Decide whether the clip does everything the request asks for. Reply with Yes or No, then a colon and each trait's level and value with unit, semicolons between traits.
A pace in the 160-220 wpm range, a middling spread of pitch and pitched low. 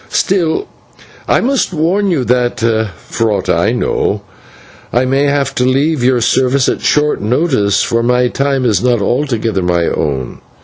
No: average, 150 wpm; average, 4.1 semitones; low, 125 Hz